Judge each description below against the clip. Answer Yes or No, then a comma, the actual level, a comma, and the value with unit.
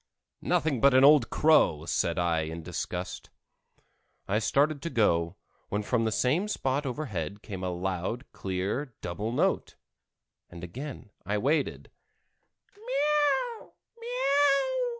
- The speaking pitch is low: Yes, low, 110 Hz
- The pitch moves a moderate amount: No, wide, 7.6 semitones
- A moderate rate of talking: No, slow, 115 wpm